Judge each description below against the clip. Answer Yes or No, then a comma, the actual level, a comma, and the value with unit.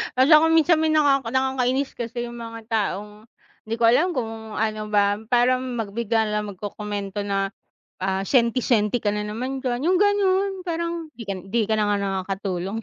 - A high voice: Yes, high, 230 Hz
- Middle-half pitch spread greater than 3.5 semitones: Yes, average, 4.1 semitones